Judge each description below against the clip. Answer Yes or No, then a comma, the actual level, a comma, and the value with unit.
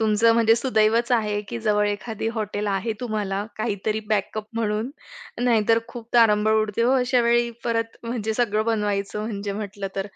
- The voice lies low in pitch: No, high, 215 Hz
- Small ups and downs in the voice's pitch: Yes, narrow, 1.8 semitones